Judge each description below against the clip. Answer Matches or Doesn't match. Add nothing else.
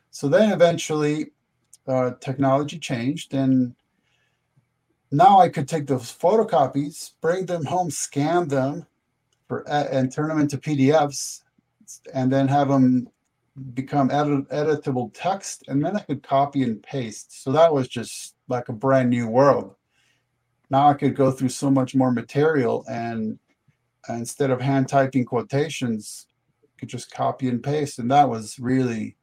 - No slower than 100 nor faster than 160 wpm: Matches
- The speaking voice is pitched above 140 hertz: Doesn't match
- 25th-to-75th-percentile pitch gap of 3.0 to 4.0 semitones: Doesn't match